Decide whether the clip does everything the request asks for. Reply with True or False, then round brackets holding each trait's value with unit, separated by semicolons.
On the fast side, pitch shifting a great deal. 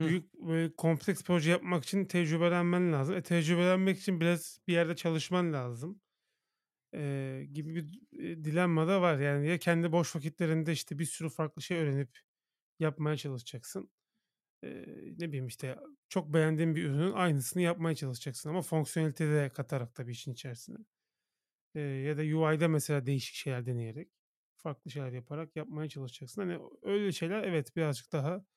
False (155 wpm; 3.2 semitones)